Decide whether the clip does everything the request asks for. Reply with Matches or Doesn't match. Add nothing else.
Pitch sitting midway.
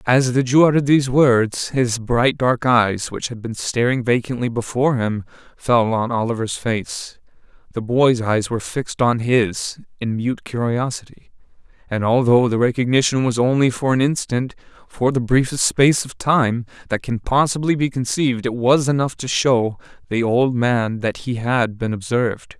Doesn't match